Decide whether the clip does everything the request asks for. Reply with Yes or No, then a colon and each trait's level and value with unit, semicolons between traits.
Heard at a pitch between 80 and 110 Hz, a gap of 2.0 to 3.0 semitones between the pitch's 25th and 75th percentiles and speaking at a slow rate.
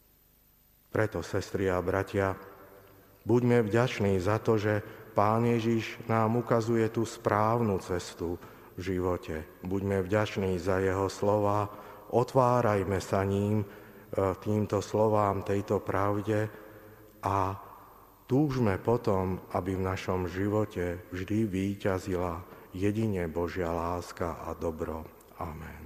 Yes: low, 100 Hz; average, 2.7 semitones; slow, 105 wpm